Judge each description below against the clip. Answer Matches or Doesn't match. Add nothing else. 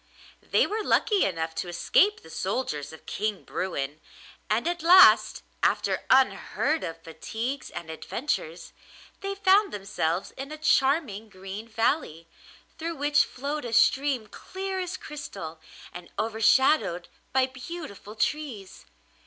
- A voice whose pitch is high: Matches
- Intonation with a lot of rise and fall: Matches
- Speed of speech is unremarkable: Doesn't match